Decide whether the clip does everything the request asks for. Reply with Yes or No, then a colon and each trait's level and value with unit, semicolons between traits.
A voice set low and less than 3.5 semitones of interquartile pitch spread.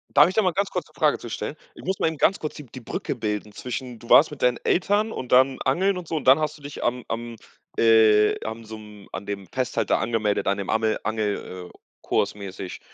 No: low, 120 Hz; wide, 5.7 semitones